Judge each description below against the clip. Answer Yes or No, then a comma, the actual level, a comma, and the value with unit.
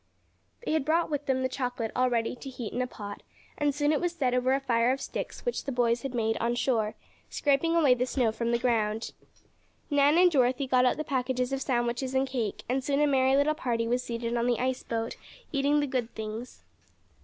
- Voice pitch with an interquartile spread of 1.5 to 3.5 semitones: Yes, average, 2.7 semitones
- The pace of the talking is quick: Yes, fast, 225 wpm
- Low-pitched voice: No, very high, 255 Hz